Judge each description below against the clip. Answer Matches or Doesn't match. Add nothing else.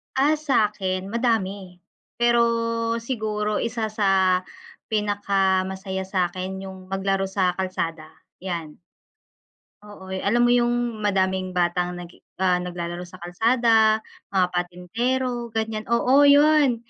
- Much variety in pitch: Doesn't match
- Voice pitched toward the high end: Matches